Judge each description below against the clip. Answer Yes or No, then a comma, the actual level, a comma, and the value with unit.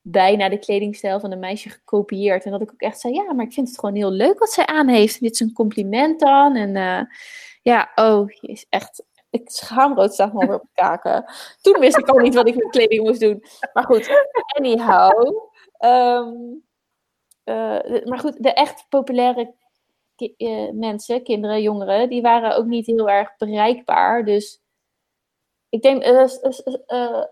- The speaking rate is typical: Yes, average, 185 wpm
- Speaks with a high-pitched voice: Yes, high, 235 Hz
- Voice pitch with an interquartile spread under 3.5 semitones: No, average, 4.2 semitones